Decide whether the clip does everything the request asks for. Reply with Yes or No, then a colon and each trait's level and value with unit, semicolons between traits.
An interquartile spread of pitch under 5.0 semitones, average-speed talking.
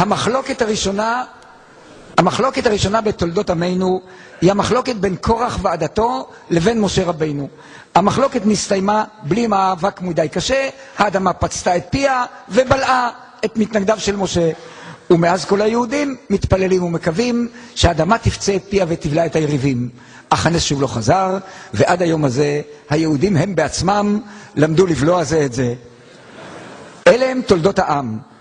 No: average, 5.3 semitones; average, 130 wpm